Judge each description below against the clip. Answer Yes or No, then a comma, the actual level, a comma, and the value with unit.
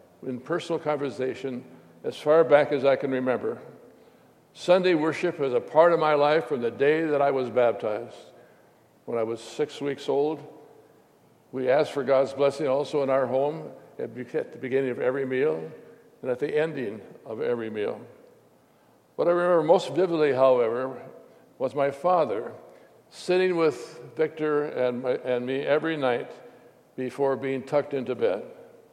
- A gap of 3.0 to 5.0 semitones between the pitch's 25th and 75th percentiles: Yes, average, 3.3 semitones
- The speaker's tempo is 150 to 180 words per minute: Yes, average, 160 wpm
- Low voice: No, medium, 145 Hz